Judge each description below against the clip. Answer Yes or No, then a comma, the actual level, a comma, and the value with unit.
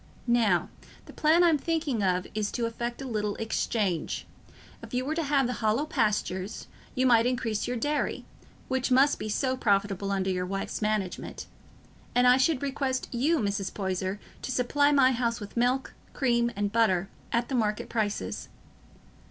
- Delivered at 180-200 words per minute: No, average, 170 wpm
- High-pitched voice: Yes, high, 235 Hz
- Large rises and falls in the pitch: No, average, 4.1 semitones